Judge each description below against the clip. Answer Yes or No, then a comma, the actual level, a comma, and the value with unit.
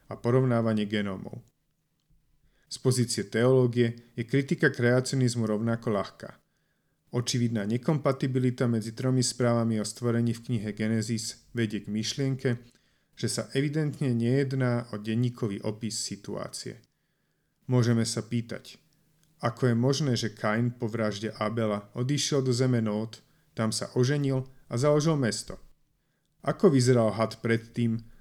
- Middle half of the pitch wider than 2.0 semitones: Yes, average, 2.9 semitones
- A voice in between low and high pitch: No, low, 120 Hz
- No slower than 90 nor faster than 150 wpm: Yes, average, 120 wpm